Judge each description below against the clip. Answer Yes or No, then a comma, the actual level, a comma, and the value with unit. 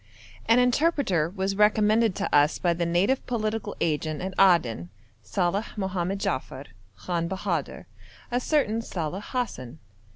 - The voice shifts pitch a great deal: No, average, 4.7 semitones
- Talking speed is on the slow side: Yes, slow, 130 wpm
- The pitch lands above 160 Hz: Yes, high, 190 Hz